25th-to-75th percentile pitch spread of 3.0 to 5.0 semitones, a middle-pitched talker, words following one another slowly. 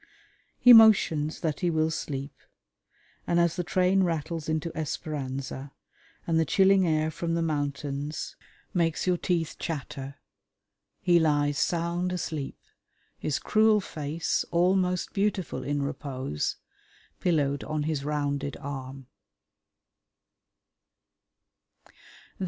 Yes: average, 3.5 semitones; medium, 155 Hz; slow, 105 wpm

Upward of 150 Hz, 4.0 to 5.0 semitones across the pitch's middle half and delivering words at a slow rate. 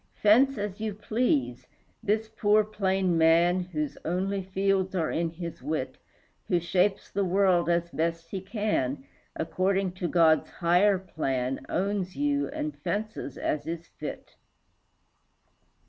No: medium, 185 Hz; average, 3.6 semitones; slow, 130 wpm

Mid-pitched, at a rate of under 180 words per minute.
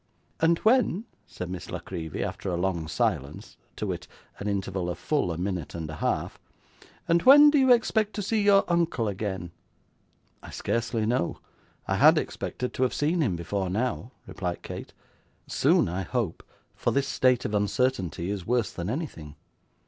No: low, 105 Hz; average, 170 wpm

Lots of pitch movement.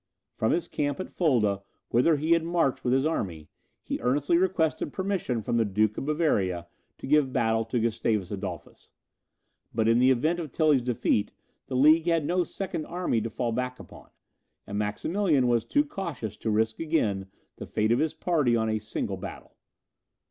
Yes: wide, 6.5 semitones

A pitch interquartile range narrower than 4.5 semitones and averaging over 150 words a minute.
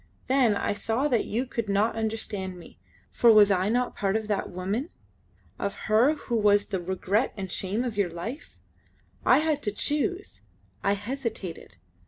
Yes: average, 3.7 semitones; average, 170 wpm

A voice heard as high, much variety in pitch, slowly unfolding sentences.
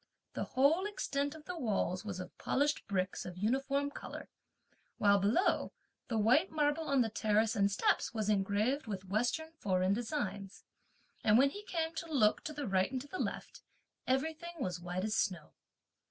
No: high, 230 Hz; wide, 6.6 semitones; average, 175 wpm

